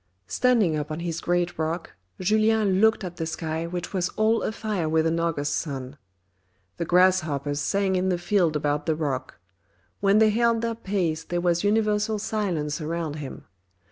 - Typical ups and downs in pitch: Yes, average, 4.7 semitones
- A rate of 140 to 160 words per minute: No, average, 170 wpm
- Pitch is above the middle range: No, medium, 175 Hz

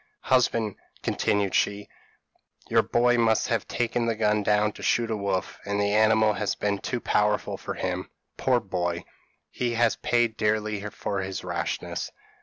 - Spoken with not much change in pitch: Yes, narrow, 2.2 semitones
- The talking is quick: No, average, 160 wpm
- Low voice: Yes, low, 105 Hz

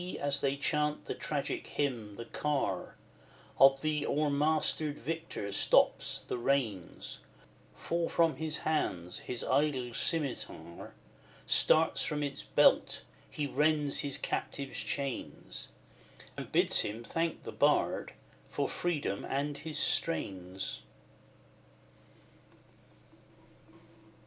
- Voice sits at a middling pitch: Yes, medium, 145 Hz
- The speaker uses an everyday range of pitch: Yes, average, 3.5 semitones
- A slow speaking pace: Yes, slow, 105 wpm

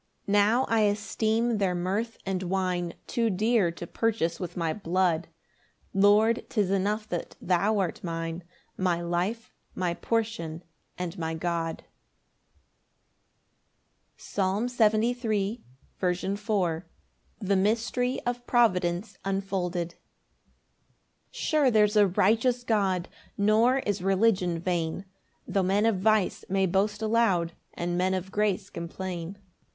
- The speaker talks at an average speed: No, slow, 120 wpm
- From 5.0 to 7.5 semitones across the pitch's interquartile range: No, average, 3.6 semitones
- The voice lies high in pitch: Yes, high, 195 Hz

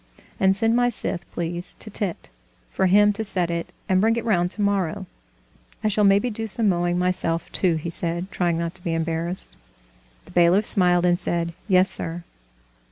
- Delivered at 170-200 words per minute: Yes, average, 180 wpm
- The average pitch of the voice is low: No, medium, 180 Hz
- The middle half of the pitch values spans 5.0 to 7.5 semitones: No, average, 2.9 semitones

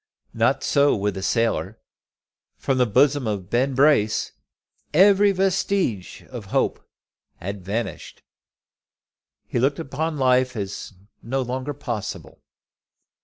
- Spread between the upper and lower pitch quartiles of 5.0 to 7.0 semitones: Yes, average, 5.3 semitones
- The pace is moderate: No, slow, 115 wpm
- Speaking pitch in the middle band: No, low, 130 Hz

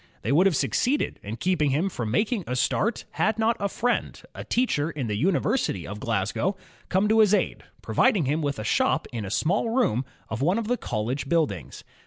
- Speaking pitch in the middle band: Yes, medium, 165 Hz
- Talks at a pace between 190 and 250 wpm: Yes, fast, 205 wpm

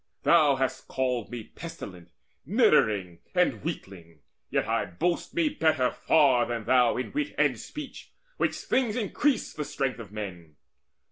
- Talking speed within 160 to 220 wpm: No, average, 145 wpm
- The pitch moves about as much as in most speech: No, wide, 8.3 semitones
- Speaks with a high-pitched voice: No, low, 125 Hz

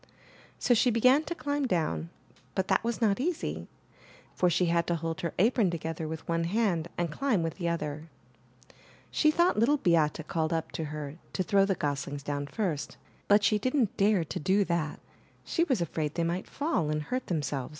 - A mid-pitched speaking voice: Yes, medium, 170 Hz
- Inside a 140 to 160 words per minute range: No, average, 190 wpm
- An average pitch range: No, wide, 6.0 semitones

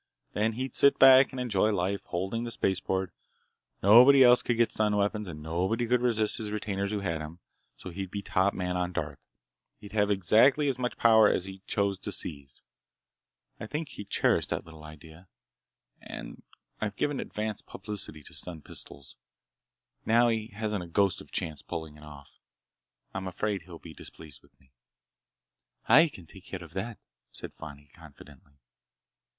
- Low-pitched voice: Yes, low, 100 Hz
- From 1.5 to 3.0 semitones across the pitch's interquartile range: No, average, 4.8 semitones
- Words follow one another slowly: No, average, 175 wpm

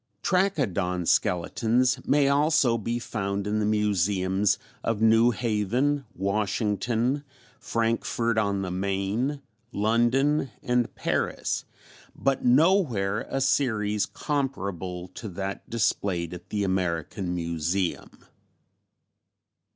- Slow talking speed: Yes, slow, 95 wpm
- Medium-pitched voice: No, low, 105 Hz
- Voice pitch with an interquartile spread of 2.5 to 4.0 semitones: No, average, 4.4 semitones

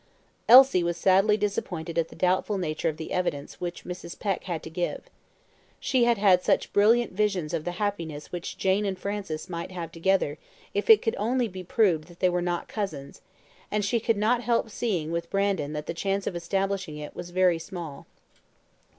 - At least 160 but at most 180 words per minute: No, average, 195 wpm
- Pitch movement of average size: Yes, average, 3.5 semitones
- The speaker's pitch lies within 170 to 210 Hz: Yes, medium, 185 Hz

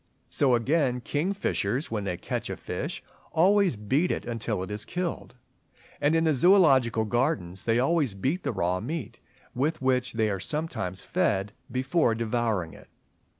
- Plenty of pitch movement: Yes, wide, 6.6 semitones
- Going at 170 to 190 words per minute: No, average, 155 wpm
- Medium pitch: No, low, 125 Hz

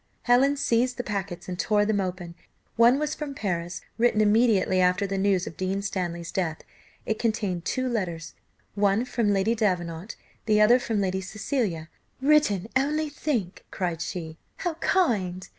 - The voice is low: No, high, 205 Hz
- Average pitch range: Yes, average, 4.8 semitones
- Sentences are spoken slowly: No, average, 160 wpm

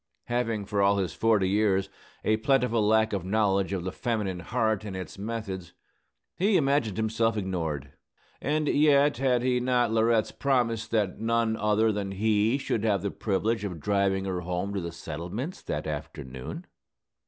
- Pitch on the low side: Yes, low, 105 Hz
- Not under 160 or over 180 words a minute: Yes, average, 165 wpm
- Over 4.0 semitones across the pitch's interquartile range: No, average, 3.3 semitones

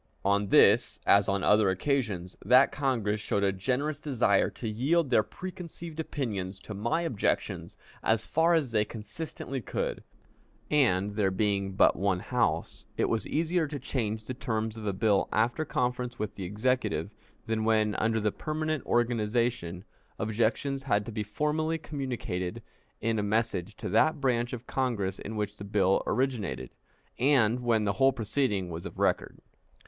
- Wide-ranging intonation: No, average, 4.5 semitones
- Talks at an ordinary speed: Yes, average, 160 wpm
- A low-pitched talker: Yes, low, 110 Hz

